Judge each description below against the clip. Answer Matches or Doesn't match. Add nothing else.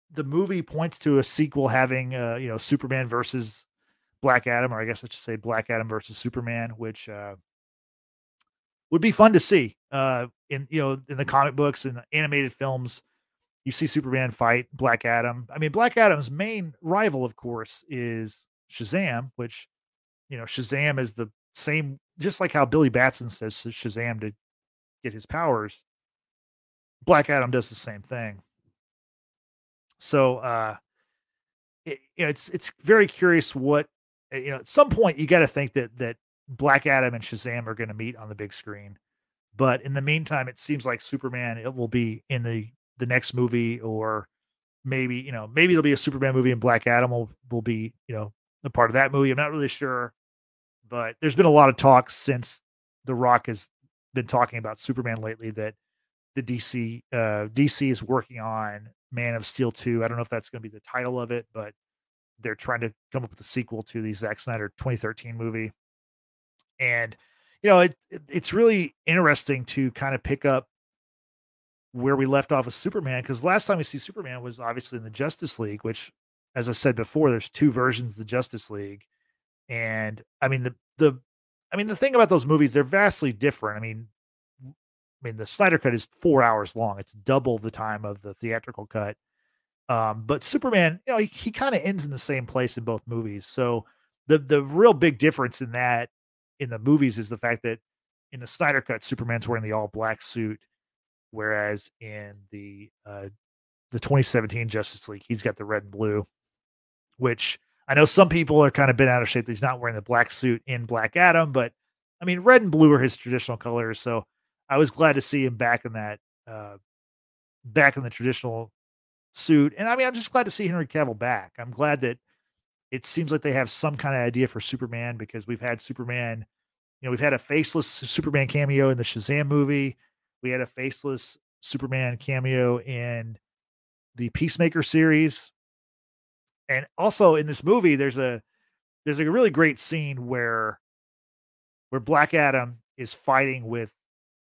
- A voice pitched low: Matches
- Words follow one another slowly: Doesn't match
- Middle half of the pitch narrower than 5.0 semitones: Matches